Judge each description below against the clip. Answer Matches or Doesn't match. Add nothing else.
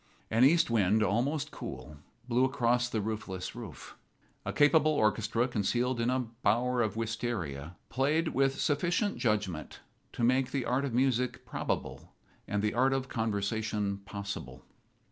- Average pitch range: Matches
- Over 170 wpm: Doesn't match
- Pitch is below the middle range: Matches